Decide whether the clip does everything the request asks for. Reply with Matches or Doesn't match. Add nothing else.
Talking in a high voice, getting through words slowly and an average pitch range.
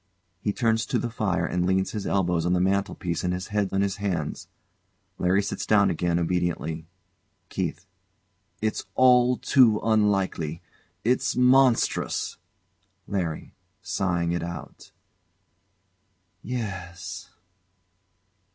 Doesn't match